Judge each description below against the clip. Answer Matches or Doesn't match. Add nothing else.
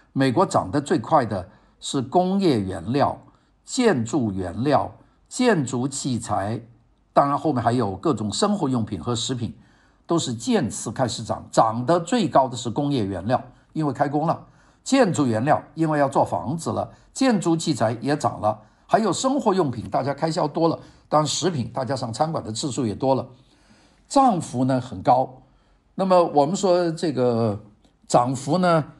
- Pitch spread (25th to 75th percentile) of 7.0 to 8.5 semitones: Doesn't match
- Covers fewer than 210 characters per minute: Doesn't match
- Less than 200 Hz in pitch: Matches